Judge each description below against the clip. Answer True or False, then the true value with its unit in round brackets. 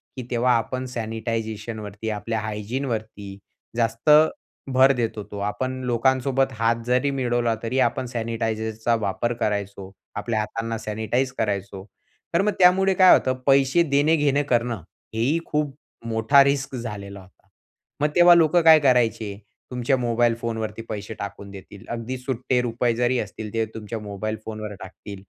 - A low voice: True (115 Hz)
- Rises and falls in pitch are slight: False (3.2 semitones)